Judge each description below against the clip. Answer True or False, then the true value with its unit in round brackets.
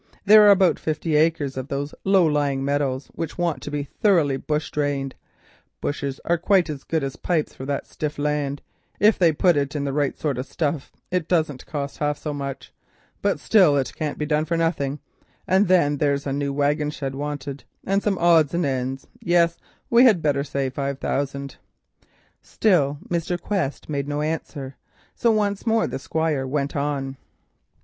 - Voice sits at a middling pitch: True (150 Hz)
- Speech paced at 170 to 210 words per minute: True (180 wpm)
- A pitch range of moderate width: True (3.3 semitones)